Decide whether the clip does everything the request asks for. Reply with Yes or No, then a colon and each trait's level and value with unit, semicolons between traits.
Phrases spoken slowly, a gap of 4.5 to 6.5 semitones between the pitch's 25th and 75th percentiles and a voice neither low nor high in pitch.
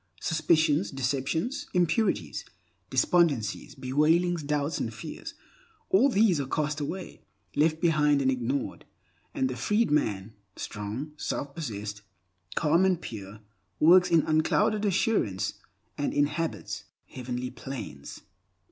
Yes: slow, 110 wpm; average, 5.2 semitones; medium, 150 Hz